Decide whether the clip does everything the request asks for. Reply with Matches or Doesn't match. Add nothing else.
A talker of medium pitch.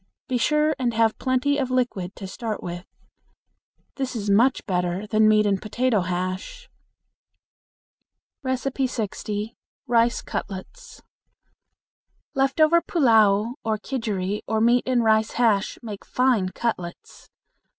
Doesn't match